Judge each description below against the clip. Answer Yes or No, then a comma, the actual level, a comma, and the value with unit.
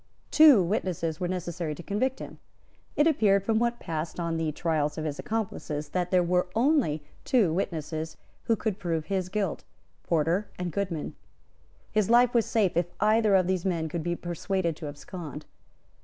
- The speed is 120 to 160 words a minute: No, average, 175 wpm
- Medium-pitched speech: Yes, medium, 180 Hz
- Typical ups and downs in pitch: Yes, average, 4.6 semitones